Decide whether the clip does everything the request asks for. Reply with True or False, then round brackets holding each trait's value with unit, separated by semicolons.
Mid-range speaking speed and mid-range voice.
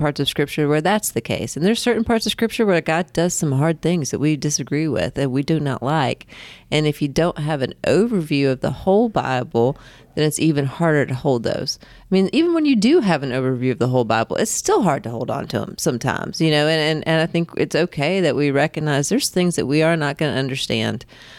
False (250 wpm; 155 Hz)